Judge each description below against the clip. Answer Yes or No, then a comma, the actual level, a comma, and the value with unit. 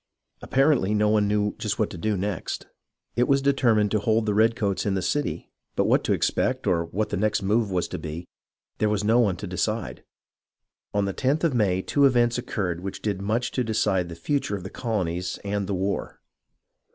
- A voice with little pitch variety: No, average, 3.2 semitones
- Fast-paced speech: Yes, fast, 210 wpm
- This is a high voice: No, low, 105 Hz